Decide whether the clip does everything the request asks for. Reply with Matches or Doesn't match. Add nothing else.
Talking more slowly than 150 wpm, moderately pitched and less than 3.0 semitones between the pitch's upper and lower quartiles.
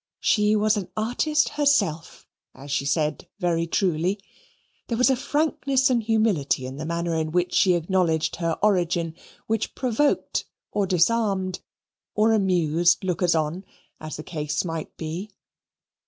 Doesn't match